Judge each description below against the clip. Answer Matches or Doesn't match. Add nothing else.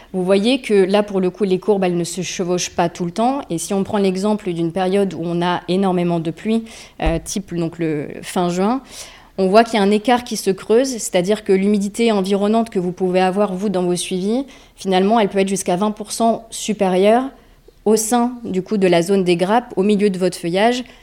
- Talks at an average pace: Doesn't match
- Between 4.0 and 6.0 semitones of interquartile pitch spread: Doesn't match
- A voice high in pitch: Matches